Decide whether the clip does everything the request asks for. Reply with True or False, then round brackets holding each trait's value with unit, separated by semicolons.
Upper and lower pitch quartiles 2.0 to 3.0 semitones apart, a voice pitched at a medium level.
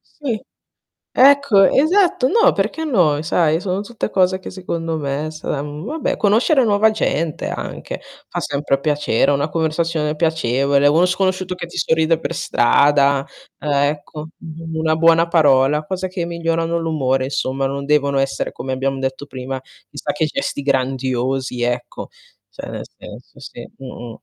False (4.6 semitones; 155 Hz)